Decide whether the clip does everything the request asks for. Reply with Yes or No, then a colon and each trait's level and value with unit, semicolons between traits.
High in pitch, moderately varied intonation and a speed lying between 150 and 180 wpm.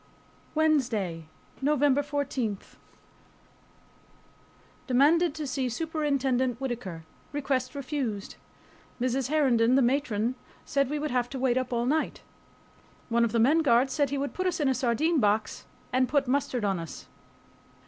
No: very high, 260 Hz; average, 3.4 semitones; average, 140 wpm